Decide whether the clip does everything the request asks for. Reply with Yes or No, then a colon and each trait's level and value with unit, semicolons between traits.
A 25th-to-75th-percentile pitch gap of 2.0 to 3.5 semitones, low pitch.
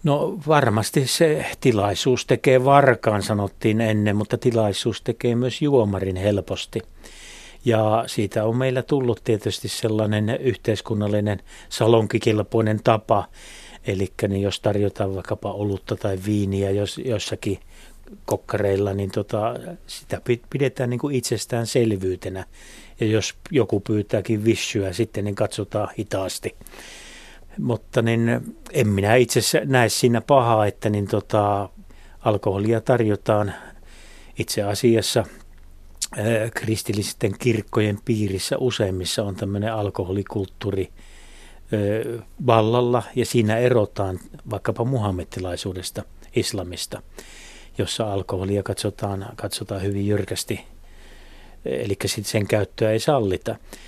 Yes: average, 2.9 semitones; low, 105 Hz